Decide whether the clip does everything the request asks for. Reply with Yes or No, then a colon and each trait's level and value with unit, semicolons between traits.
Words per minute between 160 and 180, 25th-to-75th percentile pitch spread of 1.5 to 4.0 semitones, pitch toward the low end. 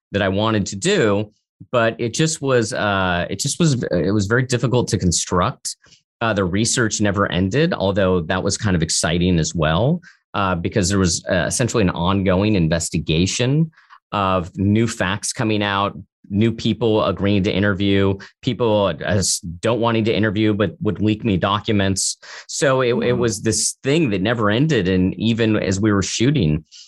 Yes: average, 170 wpm; average, 3.2 semitones; low, 105 Hz